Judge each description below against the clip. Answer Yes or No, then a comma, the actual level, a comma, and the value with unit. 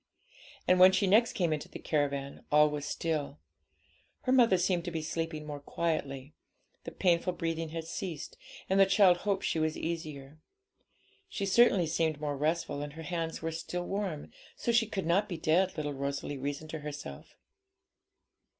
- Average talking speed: Yes, average, 170 wpm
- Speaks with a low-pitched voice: No, medium, 165 Hz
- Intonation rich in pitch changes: No, average, 3.5 semitones